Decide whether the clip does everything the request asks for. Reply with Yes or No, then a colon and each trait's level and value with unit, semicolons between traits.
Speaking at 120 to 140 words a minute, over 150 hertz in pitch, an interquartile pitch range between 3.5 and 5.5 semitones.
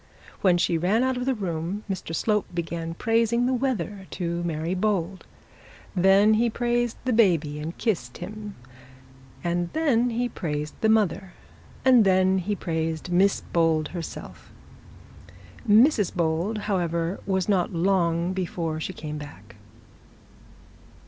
Yes: slow, 135 wpm; medium, 185 Hz; average, 4.4 semitones